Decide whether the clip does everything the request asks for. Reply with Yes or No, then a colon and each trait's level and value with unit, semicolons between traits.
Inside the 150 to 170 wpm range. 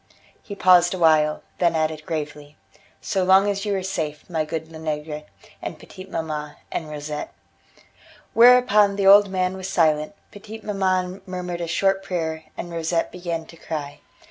Yes: average, 155 wpm